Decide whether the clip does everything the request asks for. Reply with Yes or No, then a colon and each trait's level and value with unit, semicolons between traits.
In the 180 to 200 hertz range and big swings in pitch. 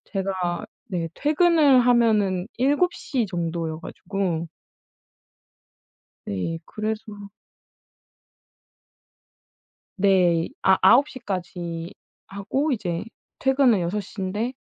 Yes: high, 195 Hz; wide, 6.0 semitones